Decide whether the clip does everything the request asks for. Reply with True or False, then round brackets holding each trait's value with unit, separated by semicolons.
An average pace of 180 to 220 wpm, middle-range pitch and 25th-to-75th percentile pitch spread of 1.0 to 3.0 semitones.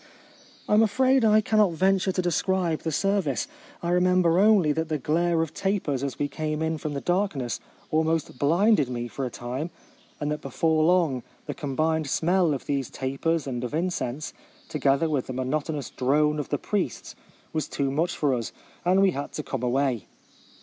False (190 wpm; 155 Hz; 4.4 semitones)